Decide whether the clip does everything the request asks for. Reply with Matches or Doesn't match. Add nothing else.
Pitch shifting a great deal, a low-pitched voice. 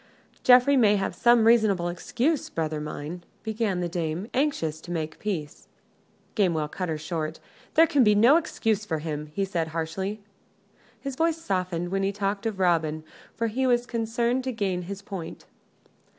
Doesn't match